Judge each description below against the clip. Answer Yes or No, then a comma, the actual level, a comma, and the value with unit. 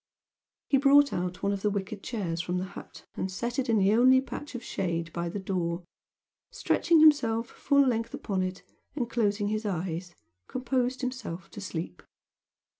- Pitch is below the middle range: No, high, 205 Hz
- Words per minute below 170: No, average, 175 wpm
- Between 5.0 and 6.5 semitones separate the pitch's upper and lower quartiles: Yes, wide, 5.5 semitones